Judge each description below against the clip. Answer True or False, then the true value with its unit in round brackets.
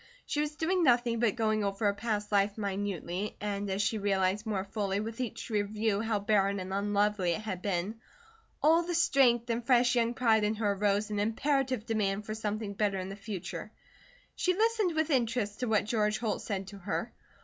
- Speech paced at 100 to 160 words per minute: False (195 wpm)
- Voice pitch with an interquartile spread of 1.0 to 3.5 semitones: True (2.9 semitones)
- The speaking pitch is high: True (215 Hz)